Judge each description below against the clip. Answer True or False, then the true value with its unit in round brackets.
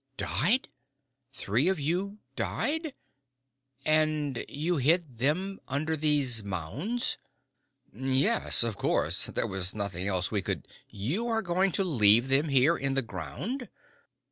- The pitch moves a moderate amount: False (8.2 semitones)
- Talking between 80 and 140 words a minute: True (135 wpm)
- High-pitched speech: False (145 Hz)